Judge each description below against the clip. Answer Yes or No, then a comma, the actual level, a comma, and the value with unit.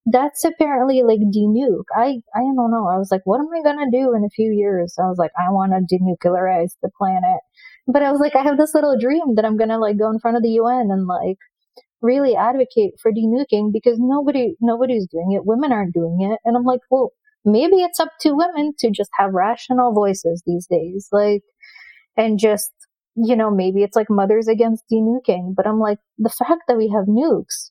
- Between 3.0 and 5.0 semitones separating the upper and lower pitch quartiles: Yes, average, 4.2 semitones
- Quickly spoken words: Yes, fast, 220 wpm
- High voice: Yes, high, 225 Hz